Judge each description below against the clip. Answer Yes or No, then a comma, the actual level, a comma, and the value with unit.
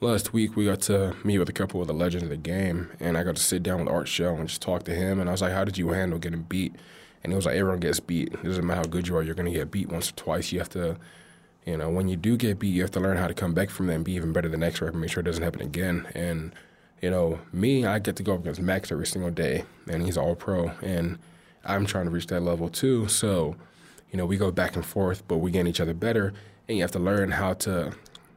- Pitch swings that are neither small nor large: No, narrow, 2.3 semitones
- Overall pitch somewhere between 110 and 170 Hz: No, very low, 90 Hz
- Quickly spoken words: Yes, fast, 300 wpm